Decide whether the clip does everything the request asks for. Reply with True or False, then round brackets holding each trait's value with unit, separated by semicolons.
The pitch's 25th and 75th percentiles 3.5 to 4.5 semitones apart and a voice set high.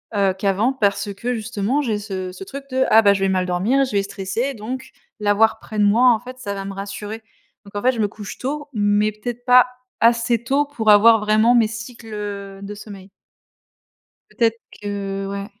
False (3.0 semitones; 215 Hz)